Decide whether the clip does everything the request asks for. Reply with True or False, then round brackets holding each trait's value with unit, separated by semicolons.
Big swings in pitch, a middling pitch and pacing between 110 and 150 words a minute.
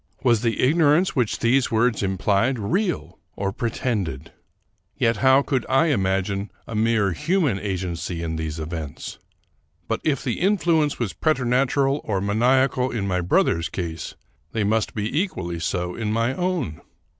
False (6.0 semitones; 115 Hz; 145 wpm)